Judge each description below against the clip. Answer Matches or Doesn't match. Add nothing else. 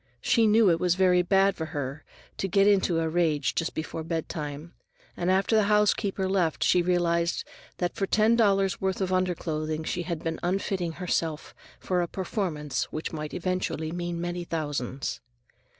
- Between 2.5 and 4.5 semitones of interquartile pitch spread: Matches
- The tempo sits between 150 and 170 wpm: Matches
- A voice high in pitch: Doesn't match